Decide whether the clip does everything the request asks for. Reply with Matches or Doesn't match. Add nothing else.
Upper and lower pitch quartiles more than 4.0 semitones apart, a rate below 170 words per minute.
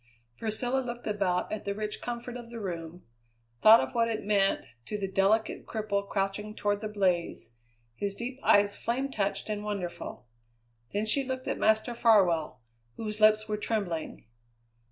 Doesn't match